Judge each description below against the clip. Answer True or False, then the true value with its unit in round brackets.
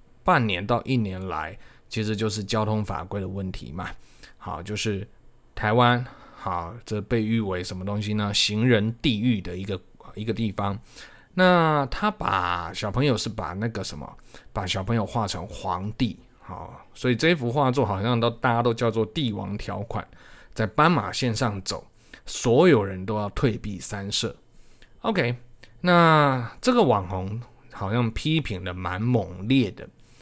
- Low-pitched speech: True (110 Hz)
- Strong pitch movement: False (3.5 semitones)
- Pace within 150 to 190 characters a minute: False (225 characters per minute)